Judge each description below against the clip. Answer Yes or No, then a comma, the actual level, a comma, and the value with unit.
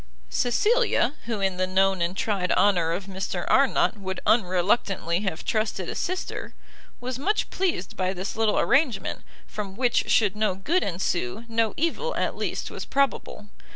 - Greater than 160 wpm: No, average, 155 wpm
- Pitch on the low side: No, high, 205 Hz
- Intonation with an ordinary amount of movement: Yes, average, 4.8 semitones